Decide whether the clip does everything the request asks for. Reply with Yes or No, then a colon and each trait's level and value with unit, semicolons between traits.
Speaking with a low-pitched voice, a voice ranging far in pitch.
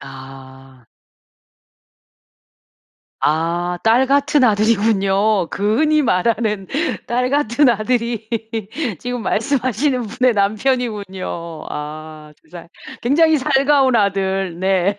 No: high, 210 Hz; wide, 5.9 semitones